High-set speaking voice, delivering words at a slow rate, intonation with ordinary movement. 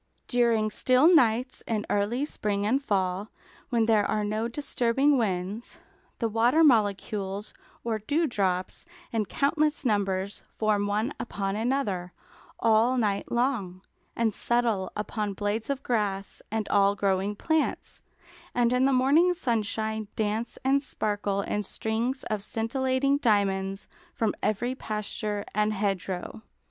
Yes: high, 220 Hz; slow, 130 wpm; average, 3.4 semitones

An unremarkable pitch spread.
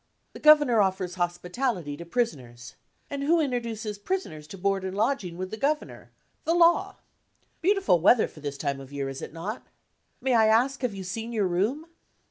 No: wide, 6.9 semitones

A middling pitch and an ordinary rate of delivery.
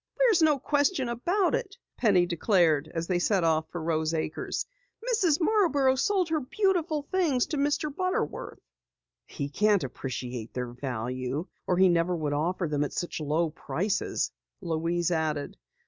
Yes: medium, 180 Hz; average, 150 wpm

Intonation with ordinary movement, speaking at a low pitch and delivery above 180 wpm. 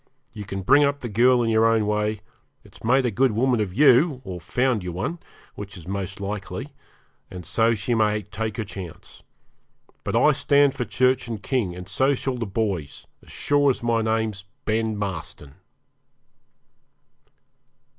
No: average, 4.4 semitones; low, 110 Hz; average, 170 wpm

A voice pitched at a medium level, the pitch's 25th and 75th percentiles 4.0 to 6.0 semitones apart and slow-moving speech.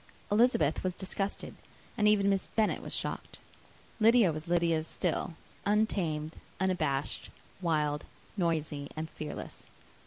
Yes: medium, 175 Hz; average, 4.7 semitones; slow, 115 wpm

